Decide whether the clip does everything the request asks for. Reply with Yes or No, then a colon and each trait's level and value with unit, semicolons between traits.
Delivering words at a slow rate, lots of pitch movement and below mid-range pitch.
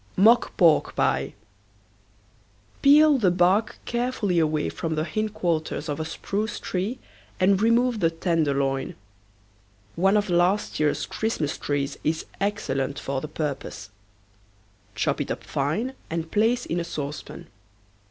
No: slow, 130 wpm; wide, 5.8 semitones; medium, 170 Hz